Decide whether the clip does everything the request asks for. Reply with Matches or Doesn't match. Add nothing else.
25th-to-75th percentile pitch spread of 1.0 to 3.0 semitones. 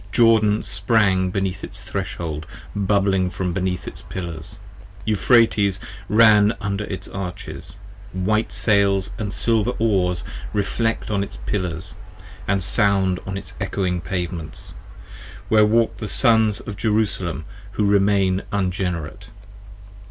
Matches